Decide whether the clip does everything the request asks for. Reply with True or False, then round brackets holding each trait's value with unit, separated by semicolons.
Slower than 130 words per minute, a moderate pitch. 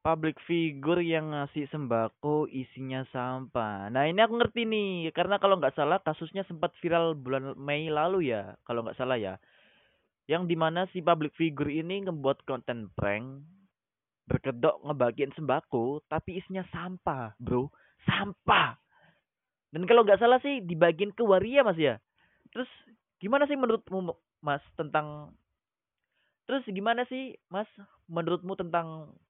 False (135 wpm; 160 Hz)